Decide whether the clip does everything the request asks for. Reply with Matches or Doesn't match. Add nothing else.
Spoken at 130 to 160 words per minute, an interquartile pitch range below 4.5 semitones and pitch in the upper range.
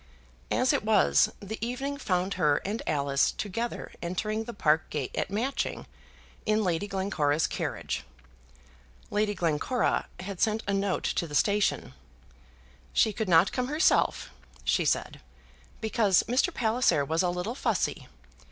Doesn't match